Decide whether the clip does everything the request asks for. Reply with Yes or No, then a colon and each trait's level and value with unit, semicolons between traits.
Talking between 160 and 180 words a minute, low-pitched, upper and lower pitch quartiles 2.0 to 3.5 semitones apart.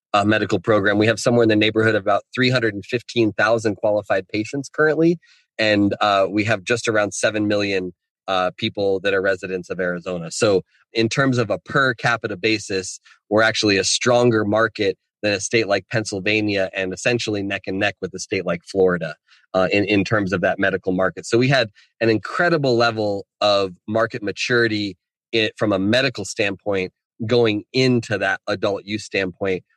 Yes: average, 175 wpm; low, 105 Hz; average, 2.7 semitones